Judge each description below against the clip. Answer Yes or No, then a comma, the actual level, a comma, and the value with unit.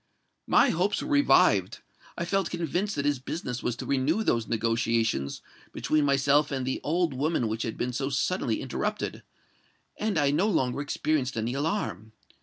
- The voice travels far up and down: Yes, wide, 5.7 semitones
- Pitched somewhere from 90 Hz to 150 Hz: Yes, medium, 140 Hz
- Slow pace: No, average, 160 wpm